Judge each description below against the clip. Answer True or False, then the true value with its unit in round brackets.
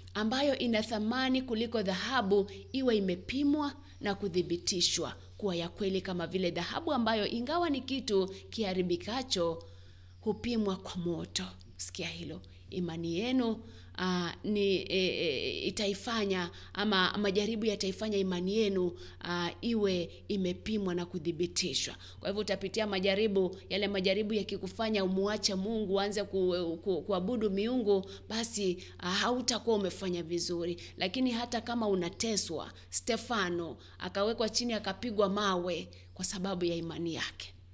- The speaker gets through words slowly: True (120 wpm)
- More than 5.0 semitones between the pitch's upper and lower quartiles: False (4.0 semitones)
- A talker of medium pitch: False (195 Hz)